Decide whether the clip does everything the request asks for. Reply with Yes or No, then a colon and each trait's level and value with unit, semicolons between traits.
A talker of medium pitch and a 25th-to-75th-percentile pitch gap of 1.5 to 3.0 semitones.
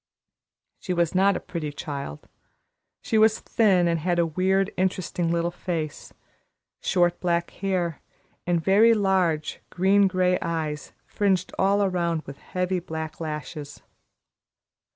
Yes: medium, 175 Hz; average, 2.7 semitones